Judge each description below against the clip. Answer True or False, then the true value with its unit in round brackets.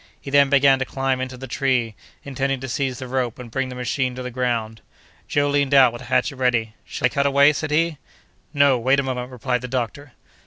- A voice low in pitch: True (130 Hz)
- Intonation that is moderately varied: False (1.9 semitones)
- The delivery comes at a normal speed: False (230 wpm)